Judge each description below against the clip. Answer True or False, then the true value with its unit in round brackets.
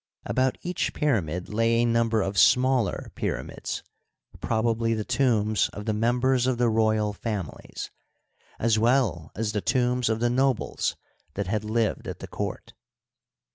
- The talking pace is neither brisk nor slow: True (145 wpm)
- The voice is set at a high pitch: False (115 Hz)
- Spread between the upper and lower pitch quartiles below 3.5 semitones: True (2.5 semitones)